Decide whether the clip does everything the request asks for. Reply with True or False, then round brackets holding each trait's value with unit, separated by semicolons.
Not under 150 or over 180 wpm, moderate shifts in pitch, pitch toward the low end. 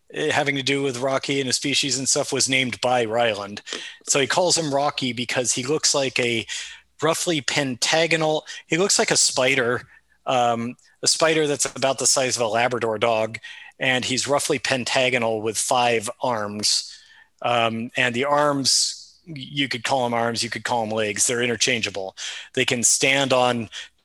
True (170 wpm; 3.0 semitones; 130 Hz)